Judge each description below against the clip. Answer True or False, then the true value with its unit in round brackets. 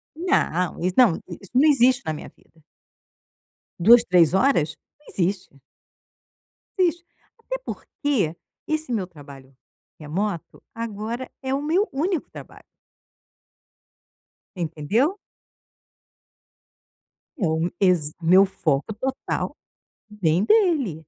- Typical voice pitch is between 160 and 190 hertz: False (205 Hz)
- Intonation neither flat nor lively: False (8.6 semitones)